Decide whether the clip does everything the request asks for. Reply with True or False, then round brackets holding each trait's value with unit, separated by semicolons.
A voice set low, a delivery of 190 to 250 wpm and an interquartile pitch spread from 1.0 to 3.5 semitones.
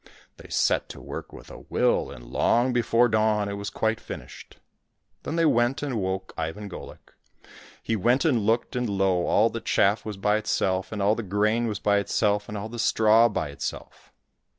True (105 Hz; 195 wpm; 2.5 semitones)